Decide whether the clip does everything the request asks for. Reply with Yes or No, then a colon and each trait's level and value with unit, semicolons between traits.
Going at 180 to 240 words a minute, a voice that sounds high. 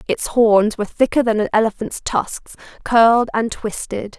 No: average, 160 wpm; high, 220 Hz